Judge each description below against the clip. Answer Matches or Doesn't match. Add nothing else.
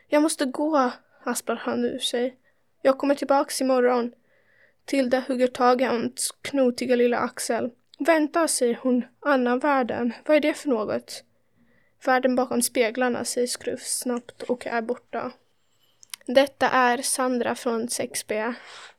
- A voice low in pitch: Doesn't match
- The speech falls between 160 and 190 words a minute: Doesn't match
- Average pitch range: Doesn't match